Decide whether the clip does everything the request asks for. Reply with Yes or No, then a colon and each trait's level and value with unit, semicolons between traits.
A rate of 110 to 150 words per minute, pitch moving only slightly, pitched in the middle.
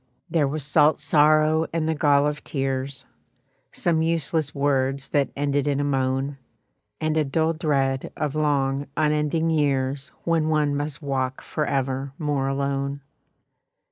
Yes: average, 140 wpm; narrow, 2.1 semitones; medium, 145 Hz